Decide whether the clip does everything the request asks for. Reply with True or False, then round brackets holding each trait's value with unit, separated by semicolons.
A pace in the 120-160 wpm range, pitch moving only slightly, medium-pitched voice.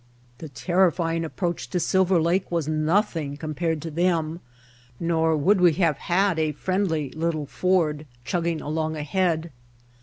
True (140 wpm; 2.3 semitones; 165 Hz)